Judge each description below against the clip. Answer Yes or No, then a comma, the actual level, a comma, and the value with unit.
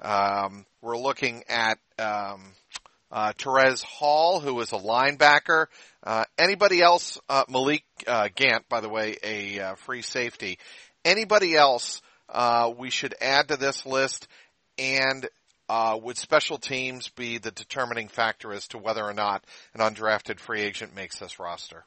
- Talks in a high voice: No, low, 120 Hz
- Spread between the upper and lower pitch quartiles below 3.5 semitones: No, average, 4.1 semitones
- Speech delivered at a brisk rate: No, average, 155 wpm